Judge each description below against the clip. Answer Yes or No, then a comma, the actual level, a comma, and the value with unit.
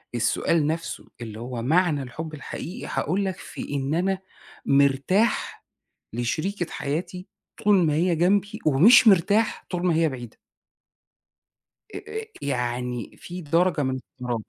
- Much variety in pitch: Yes, wide, 5.7 semitones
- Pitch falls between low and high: Yes, medium, 160 Hz